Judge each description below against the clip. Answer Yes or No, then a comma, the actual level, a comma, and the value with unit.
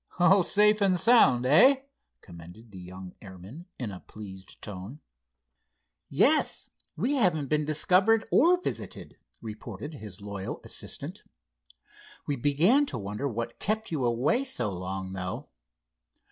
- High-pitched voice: No, low, 125 Hz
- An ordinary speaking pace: No, slow, 130 wpm